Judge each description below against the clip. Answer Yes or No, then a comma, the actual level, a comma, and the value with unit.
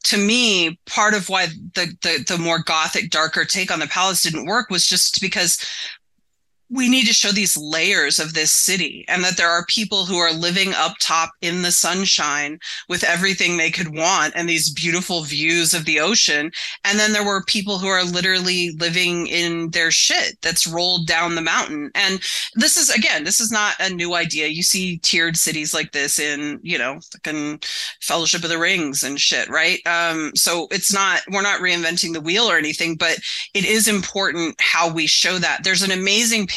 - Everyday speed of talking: Yes, average, 195 wpm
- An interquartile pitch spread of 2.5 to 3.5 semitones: Yes, average, 2.9 semitones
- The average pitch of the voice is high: No, medium, 175 Hz